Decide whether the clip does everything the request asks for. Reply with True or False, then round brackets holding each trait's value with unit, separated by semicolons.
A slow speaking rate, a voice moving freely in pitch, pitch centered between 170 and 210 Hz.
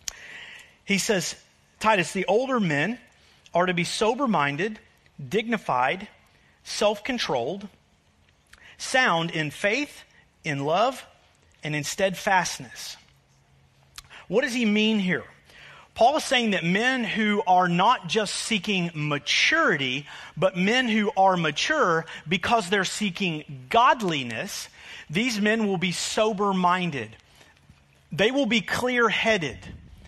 True (115 wpm; 5.8 semitones; 190 Hz)